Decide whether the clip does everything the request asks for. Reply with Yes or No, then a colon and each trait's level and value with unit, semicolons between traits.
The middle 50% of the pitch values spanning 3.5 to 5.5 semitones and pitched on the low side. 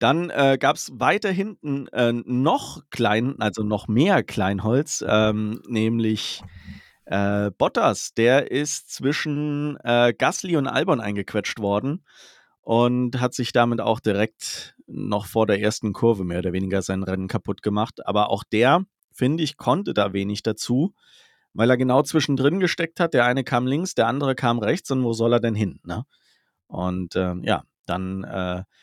Yes: average, 4.9 semitones; low, 115 Hz